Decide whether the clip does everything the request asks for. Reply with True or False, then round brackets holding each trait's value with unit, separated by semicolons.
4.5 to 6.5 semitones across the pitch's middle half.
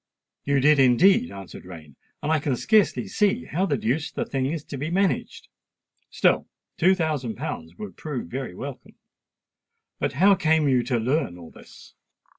True (5.1 semitones)